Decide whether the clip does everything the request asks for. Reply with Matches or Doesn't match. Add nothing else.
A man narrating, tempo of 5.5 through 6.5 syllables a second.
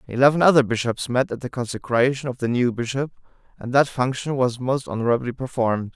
Matches